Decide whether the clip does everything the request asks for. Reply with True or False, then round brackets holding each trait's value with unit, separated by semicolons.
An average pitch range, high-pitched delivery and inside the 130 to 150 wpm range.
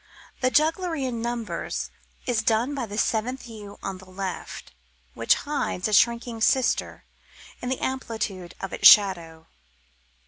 True (4.4 semitones; 230 Hz; 140 wpm)